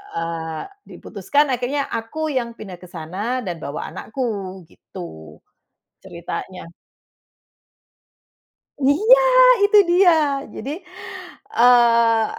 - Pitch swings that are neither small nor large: No, wide, 6.9 semitones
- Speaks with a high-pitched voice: Yes, high, 230 Hz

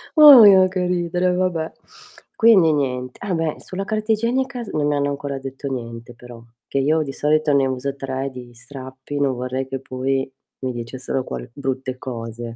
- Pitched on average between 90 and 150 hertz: Yes, medium, 140 Hz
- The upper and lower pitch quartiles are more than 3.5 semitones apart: Yes, average, 5.0 semitones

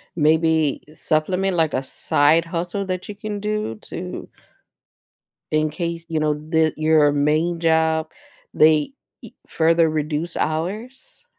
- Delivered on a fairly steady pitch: Yes, narrow, 2.2 semitones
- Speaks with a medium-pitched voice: Yes, medium, 160 Hz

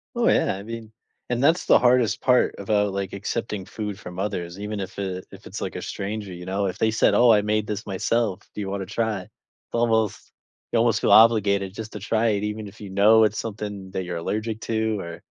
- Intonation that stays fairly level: Yes, narrow, 2.3 semitones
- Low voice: Yes, low, 105 Hz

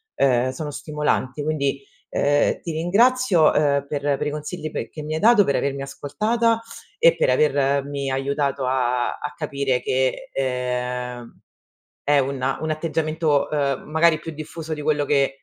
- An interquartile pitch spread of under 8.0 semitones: Yes, narrow, 2.6 semitones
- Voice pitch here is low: No, medium, 145 Hz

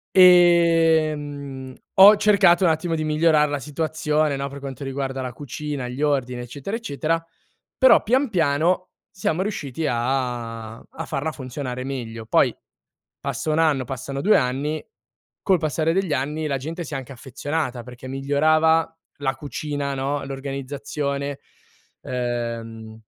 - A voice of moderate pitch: Yes, medium, 145 Hz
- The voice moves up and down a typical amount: Yes, average, 3.3 semitones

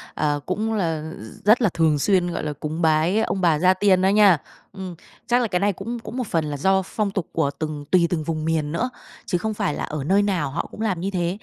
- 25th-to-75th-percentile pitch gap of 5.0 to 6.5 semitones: No, average, 4.3 semitones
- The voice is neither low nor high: Yes, medium, 180 Hz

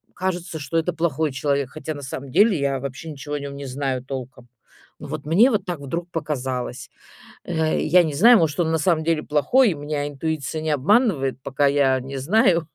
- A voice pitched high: No, medium, 150 Hz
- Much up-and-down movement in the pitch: No, average, 3.4 semitones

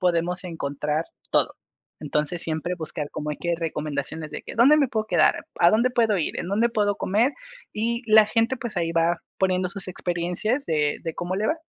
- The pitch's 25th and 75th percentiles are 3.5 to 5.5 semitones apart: Yes, average, 5.1 semitones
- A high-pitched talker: No, medium, 180 Hz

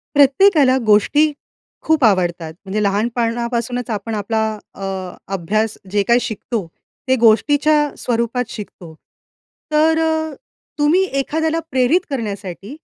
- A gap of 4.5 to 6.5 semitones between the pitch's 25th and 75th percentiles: Yes, wide, 5.6 semitones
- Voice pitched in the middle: No, high, 235 Hz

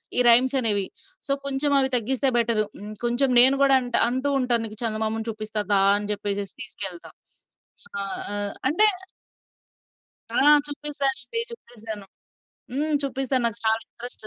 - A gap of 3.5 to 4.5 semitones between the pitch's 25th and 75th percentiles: Yes, average, 3.9 semitones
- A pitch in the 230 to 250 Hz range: Yes, high, 240 Hz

